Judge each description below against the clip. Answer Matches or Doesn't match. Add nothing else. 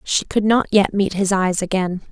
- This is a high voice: Matches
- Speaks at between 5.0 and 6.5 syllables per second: Doesn't match